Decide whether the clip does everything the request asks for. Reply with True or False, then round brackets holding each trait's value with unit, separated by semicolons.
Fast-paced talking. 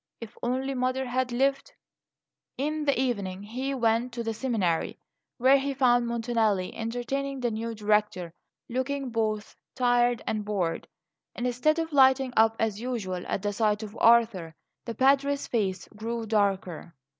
False (150 wpm)